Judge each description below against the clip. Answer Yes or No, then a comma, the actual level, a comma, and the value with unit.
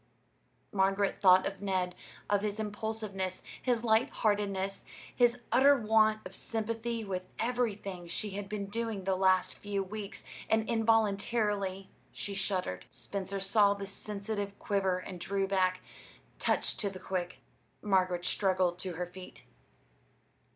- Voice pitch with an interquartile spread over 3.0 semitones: No, narrow, 2.4 semitones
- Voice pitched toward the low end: No, high, 200 Hz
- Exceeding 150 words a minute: No, slow, 135 wpm